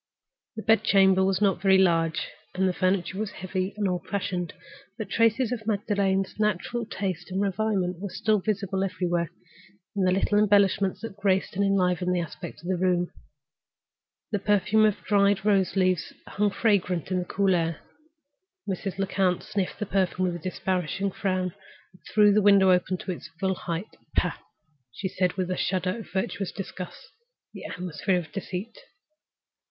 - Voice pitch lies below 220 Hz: Yes, high, 190 Hz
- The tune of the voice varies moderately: No, narrow, 1.9 semitones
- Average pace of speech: Yes, average, 165 wpm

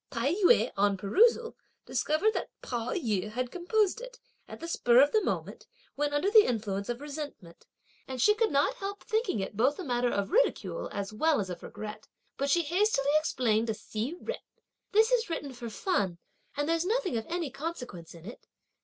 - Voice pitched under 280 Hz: No, very high, 285 Hz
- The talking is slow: No, average, 190 wpm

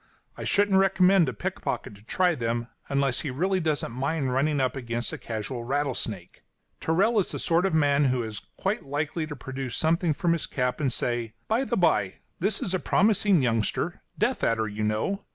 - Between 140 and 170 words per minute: No, average, 190 wpm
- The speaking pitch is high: No, medium, 140 Hz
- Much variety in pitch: Yes, wide, 6.8 semitones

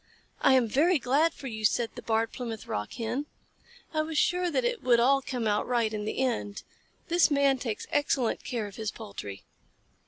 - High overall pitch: Yes, high, 245 Hz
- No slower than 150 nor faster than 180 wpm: No, average, 195 wpm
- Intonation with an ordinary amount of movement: Yes, average, 4.6 semitones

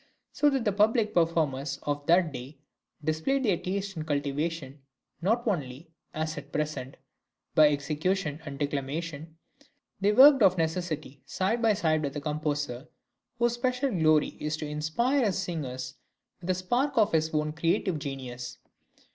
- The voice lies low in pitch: No, medium, 160 Hz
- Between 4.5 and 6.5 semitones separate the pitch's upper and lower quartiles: Yes, average, 5.1 semitones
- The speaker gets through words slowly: No, average, 155 wpm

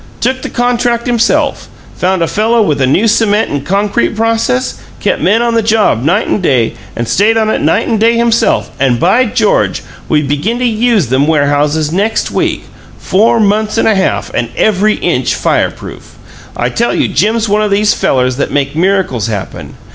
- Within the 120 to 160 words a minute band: No, average, 185 wpm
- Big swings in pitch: Yes, wide, 7.4 semitones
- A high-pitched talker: Yes, high, 210 Hz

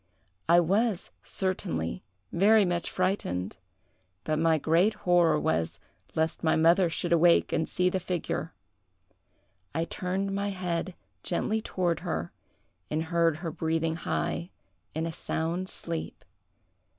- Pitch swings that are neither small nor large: No, narrow, 2.3 semitones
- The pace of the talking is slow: Yes, slow, 125 wpm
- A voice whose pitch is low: No, medium, 170 Hz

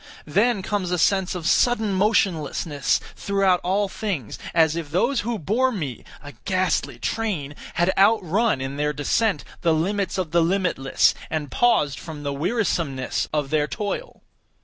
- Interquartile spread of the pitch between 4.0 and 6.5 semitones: Yes, wide, 5.5 semitones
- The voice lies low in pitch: No, medium, 180 Hz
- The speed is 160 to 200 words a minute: No, average, 150 wpm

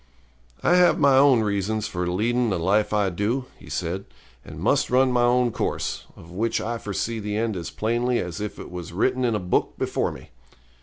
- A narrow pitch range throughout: No, average, 4.2 semitones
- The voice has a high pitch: No, low, 110 Hz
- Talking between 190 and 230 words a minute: Yes, fast, 205 wpm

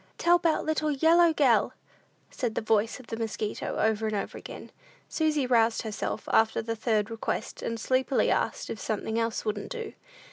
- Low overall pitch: No, high, 230 Hz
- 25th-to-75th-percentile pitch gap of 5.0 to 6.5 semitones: Yes, wide, 5.4 semitones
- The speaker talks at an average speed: Yes, average, 175 wpm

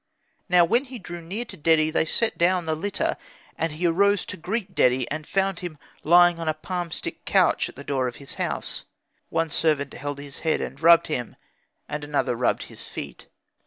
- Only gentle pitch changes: No, average, 3.5 semitones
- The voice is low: No, medium, 165 Hz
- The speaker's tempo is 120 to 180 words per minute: No, average, 200 wpm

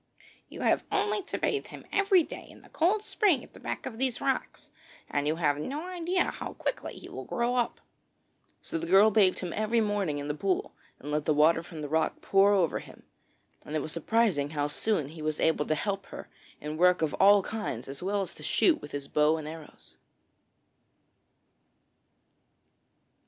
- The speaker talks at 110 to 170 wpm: No, average, 195 wpm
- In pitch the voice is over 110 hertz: Yes, medium, 185 Hz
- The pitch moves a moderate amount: No, wide, 7.5 semitones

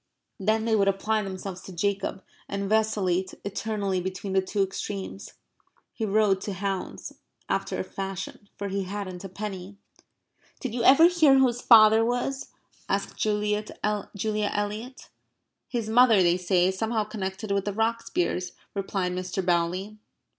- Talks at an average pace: Yes, average, 145 wpm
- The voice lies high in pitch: Yes, high, 200 Hz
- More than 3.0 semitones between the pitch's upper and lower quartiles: No, narrow, 2.5 semitones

